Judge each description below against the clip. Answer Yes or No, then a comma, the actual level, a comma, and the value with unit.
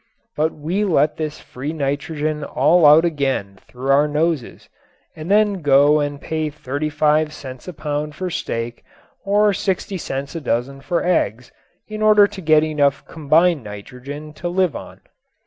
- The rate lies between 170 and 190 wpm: No, average, 155 wpm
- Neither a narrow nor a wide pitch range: Yes, average, 3.4 semitones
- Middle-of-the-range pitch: Yes, medium, 150 Hz